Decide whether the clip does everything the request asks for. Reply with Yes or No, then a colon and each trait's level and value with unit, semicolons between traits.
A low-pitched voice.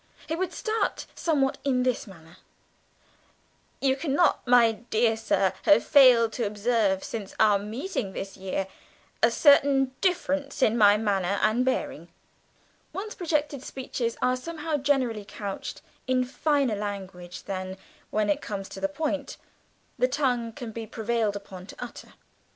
No: high, 235 Hz